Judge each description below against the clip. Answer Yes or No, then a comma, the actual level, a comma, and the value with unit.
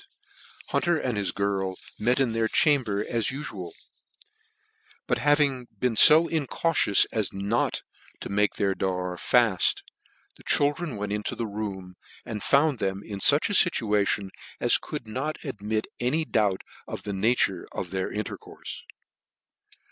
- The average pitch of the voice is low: Yes, low, 110 Hz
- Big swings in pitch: Yes, wide, 5.7 semitones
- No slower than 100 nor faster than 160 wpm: Yes, average, 155 wpm